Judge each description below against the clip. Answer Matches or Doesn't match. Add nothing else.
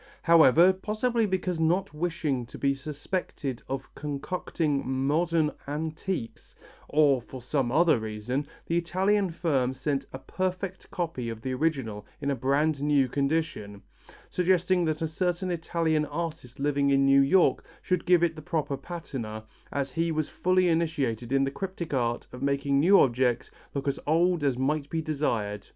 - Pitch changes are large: Doesn't match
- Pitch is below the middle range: Doesn't match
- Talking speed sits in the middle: Matches